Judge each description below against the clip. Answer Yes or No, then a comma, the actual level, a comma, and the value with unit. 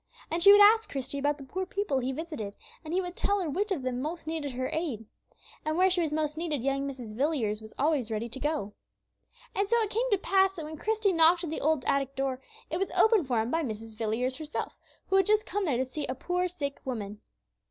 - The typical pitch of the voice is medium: No, very high, 305 Hz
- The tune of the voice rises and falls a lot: Yes, wide, 6.0 semitones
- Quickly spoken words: Yes, fast, 245 wpm